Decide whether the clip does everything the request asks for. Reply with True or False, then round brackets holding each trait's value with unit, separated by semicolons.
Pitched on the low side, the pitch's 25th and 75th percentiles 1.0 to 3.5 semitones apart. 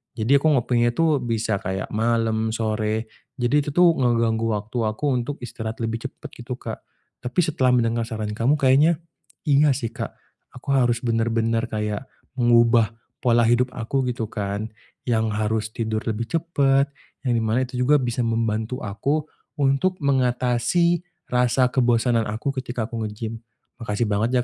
True (120 Hz; 2.7 semitones)